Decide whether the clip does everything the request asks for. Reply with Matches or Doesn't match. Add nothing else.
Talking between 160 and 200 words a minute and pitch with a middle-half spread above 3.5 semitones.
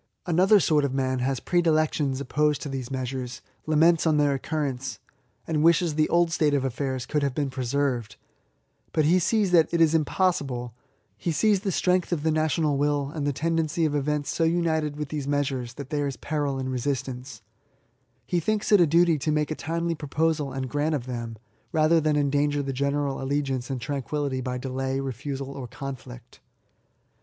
Doesn't match